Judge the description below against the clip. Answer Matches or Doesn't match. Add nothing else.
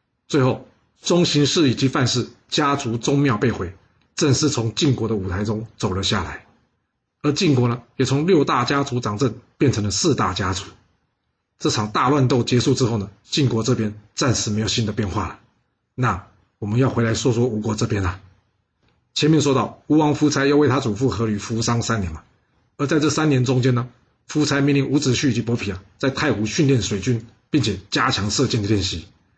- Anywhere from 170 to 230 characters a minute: Doesn't match